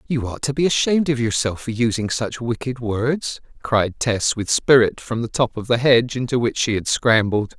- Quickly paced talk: Yes, fast, 215 wpm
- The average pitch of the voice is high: No, low, 120 Hz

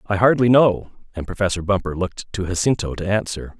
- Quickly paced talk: No, average, 185 wpm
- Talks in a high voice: No, low, 100 Hz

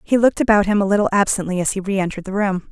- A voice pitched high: Yes, high, 200 Hz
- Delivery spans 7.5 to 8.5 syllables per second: Yes, 7.8 syllables/s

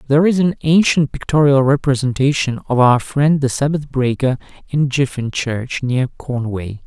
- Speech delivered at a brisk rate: No, average, 150 wpm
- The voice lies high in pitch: No, low, 135 Hz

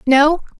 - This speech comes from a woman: Yes, female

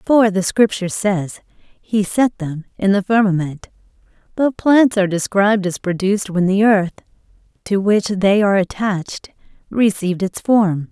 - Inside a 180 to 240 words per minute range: No, average, 150 wpm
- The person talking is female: Yes, female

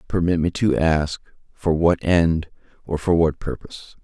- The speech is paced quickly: No, average, 165 wpm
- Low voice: Yes, very low, 80 Hz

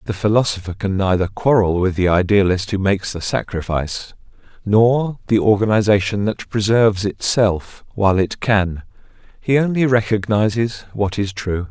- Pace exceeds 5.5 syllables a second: No, 4.9 syllables/s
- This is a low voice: Yes, low, 105 Hz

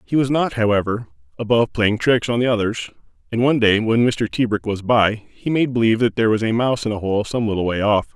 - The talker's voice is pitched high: No, low, 115 Hz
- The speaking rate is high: Yes, fast, 245 wpm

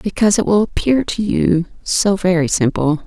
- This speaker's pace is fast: No, average, 175 wpm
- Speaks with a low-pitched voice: No, high, 190 Hz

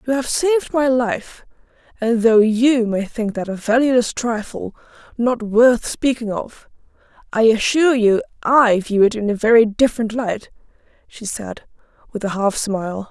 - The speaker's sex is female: Yes, female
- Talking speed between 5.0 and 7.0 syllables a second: No, 4.5 syllables/s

